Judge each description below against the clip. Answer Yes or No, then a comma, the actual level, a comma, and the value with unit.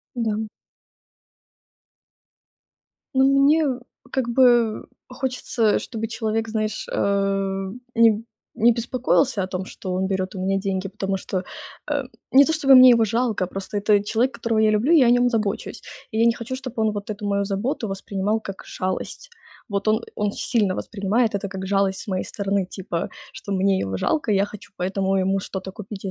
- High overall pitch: Yes, high, 210 Hz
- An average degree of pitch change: Yes, average, 3.3 semitones